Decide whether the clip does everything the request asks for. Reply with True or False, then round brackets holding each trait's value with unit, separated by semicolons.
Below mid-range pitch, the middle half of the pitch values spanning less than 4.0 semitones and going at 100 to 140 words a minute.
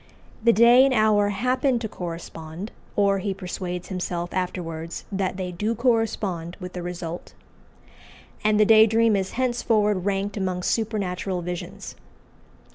False (195 Hz; 3.6 semitones; 135 wpm)